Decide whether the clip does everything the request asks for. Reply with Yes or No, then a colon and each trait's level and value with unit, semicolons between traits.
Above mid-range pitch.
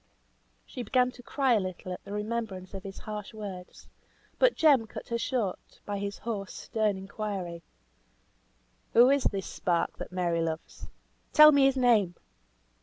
Yes: high, 210 Hz